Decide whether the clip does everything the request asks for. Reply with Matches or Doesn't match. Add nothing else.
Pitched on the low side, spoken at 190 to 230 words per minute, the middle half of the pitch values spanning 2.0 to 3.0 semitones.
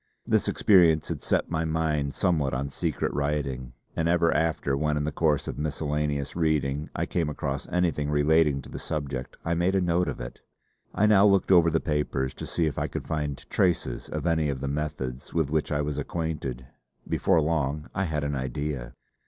Matches